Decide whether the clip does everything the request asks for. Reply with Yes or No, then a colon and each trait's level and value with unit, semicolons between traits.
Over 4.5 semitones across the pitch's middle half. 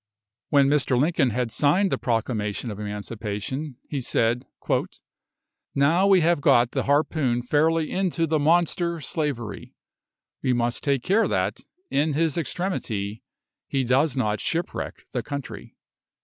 Yes: average, 5.2 semitones